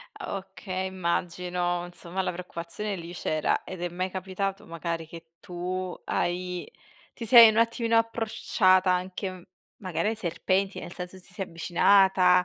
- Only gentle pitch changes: Yes, narrow, 1.7 semitones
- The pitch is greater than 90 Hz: Yes, medium, 185 Hz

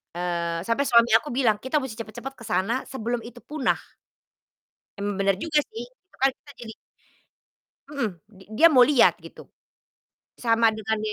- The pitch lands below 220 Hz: No, high, 230 Hz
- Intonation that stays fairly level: No, average, 3.8 semitones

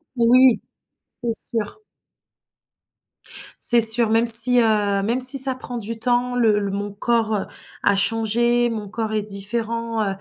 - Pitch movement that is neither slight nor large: No, narrow, 2.2 semitones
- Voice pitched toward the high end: Yes, high, 230 Hz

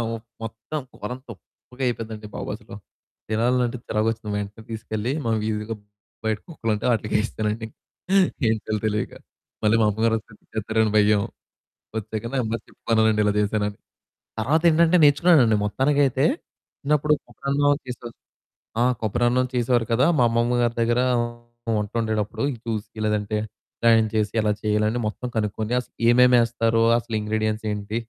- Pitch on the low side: Yes, low, 110 Hz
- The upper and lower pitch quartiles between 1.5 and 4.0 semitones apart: Yes, narrow, 2.4 semitones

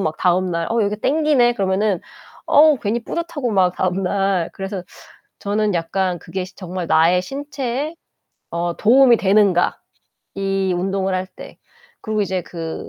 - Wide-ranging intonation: No, average, 4.0 semitones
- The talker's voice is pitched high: Yes, high, 195 Hz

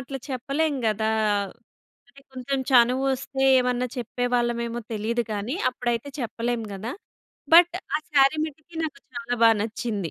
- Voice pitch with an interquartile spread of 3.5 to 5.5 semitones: No, average, 2.8 semitones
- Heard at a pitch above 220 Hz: Yes, high, 245 Hz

